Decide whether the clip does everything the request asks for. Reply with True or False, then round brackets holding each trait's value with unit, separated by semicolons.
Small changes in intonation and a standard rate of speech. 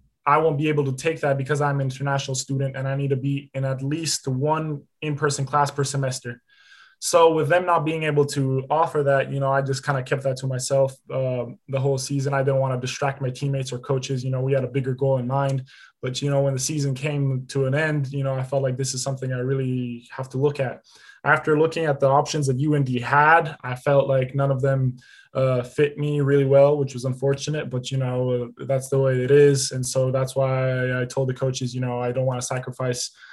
False (1.7 semitones; 245 wpm)